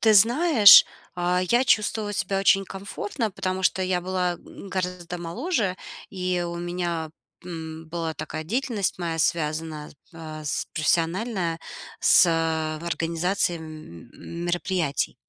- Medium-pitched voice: Yes, medium, 180 Hz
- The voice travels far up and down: No, average, 3.1 semitones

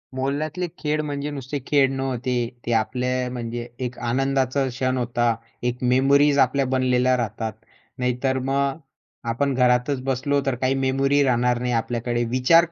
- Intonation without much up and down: Yes, narrow, 2.0 semitones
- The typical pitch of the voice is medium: No, low, 130 Hz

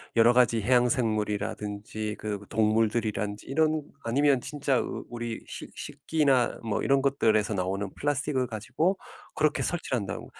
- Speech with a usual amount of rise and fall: Yes, average, 4.4 semitones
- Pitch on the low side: Yes, low, 115 Hz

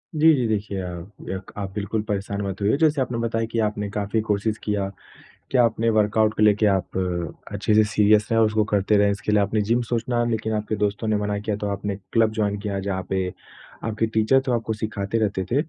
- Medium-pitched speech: No, low, 105 Hz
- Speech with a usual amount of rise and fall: No, narrow, 1.9 semitones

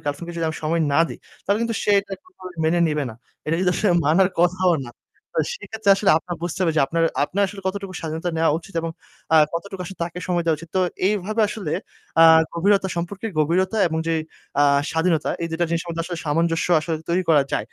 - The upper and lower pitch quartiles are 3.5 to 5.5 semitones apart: No, average, 2.8 semitones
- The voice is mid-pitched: Yes, medium, 175 Hz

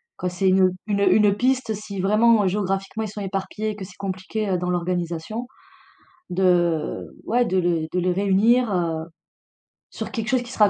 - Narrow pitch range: No, average, 3.0 semitones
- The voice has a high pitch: Yes, high, 195 Hz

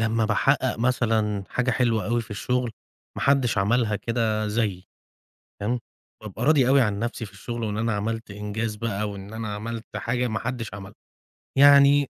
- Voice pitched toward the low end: Yes, low, 115 Hz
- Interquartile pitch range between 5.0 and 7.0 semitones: No, average, 2.7 semitones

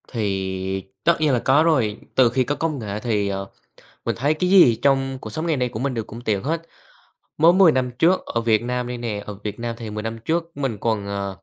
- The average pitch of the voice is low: Yes, low, 120 Hz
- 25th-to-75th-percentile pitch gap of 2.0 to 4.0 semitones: No, average, 5.3 semitones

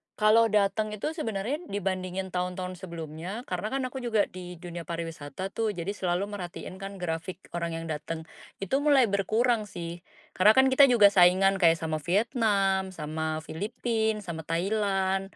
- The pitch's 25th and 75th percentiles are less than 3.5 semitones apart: No, average, 3.8 semitones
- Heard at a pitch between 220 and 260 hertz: No, high, 190 Hz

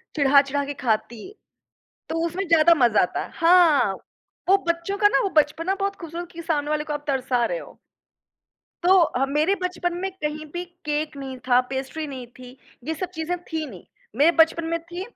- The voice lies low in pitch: No, very high, 315 Hz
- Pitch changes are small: No, average, 3.9 semitones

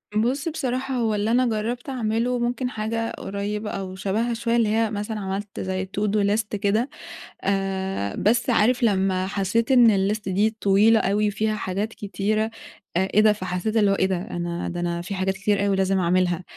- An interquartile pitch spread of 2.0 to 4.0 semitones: Yes, average, 2.9 semitones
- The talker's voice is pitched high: Yes, high, 210 Hz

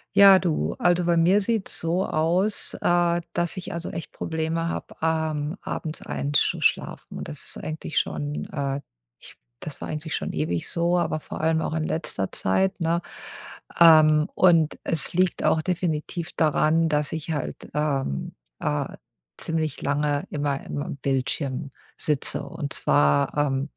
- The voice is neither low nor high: Yes, medium, 160 Hz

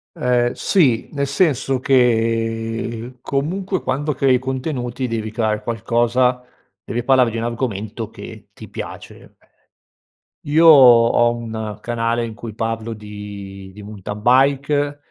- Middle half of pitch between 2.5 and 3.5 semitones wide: Yes, average, 2.9 semitones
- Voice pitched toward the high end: No, low, 120 Hz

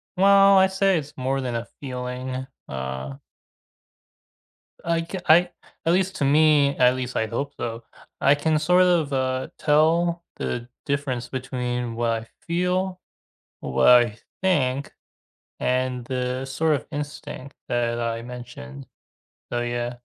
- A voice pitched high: No, low, 130 Hz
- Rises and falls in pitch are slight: No, average, 4.7 semitones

